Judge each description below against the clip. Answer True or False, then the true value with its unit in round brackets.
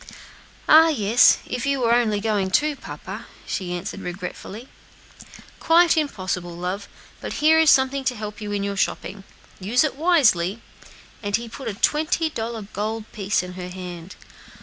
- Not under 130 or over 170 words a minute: True (165 wpm)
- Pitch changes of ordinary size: False (5.9 semitones)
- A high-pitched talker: True (215 Hz)